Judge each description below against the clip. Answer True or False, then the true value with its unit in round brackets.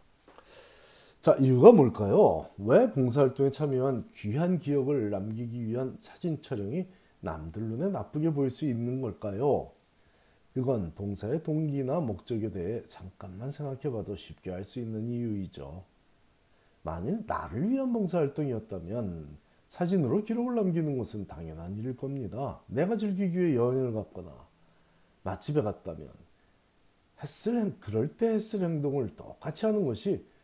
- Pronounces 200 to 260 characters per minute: False (290 characters per minute)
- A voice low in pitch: True (130 Hz)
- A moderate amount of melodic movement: False (7.4 semitones)